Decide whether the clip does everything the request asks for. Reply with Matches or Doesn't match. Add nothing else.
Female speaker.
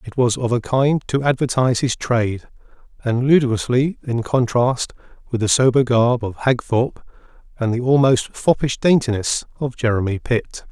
Doesn't match